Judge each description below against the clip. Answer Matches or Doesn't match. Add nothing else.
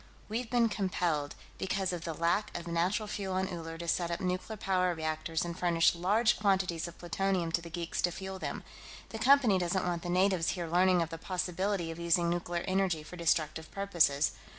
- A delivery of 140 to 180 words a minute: Doesn't match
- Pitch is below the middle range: Doesn't match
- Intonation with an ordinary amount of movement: Doesn't match